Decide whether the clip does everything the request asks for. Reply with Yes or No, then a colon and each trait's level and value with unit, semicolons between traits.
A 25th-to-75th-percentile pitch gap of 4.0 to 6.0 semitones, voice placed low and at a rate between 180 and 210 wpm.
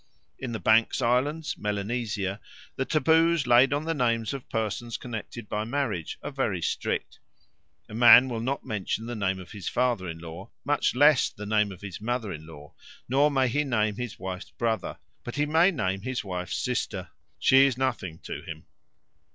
Yes: average, 4.9 semitones; low, 115 Hz; average, 185 wpm